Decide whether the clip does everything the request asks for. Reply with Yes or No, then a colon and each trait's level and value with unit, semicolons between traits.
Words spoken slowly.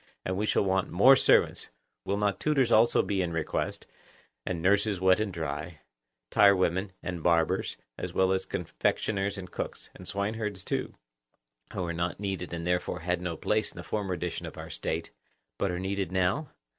No: average, 180 wpm